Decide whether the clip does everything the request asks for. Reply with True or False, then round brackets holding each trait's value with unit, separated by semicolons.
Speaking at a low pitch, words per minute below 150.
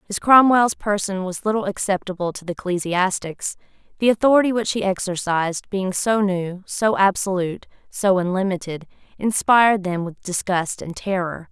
False (190 Hz; 140 wpm)